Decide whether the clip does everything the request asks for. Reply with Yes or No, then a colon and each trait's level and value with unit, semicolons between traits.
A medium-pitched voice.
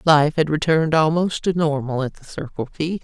Yes: medium, 155 Hz